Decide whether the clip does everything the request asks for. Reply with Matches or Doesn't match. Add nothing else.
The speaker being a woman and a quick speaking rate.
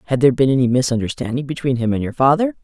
Matches